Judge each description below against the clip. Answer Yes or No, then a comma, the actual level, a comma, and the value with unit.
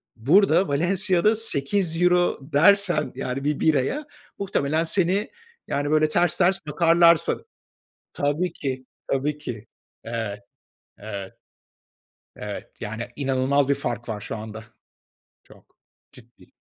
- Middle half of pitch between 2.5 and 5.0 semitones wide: No, wide, 5.6 semitones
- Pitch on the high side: No, medium, 150 Hz